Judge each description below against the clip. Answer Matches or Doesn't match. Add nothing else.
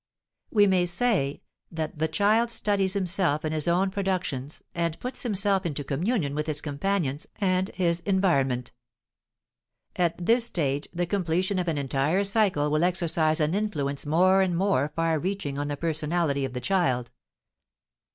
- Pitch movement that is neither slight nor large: Matches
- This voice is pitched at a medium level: Matches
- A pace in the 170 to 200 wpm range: Doesn't match